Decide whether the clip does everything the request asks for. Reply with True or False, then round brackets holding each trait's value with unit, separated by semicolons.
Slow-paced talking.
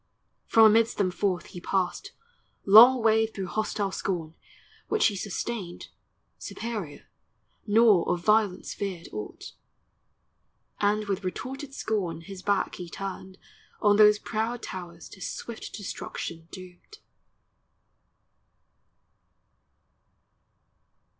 True (100 wpm)